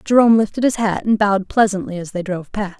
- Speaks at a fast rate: Yes, fast, 235 wpm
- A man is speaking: No, female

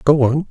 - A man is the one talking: Yes, male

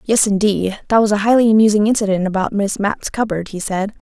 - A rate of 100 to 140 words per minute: No, fast, 205 wpm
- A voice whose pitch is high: Yes, high, 205 Hz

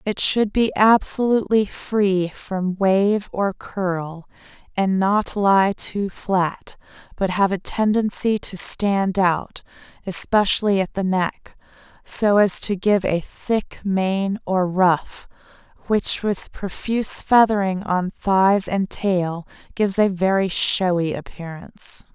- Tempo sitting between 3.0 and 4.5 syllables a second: Yes, 3.5 syllables/s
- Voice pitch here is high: Yes, high, 195 Hz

